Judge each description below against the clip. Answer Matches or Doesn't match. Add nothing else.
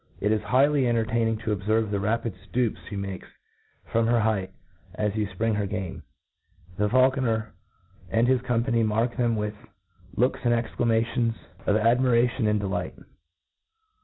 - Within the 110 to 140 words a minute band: Doesn't match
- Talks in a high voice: Doesn't match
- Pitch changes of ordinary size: Doesn't match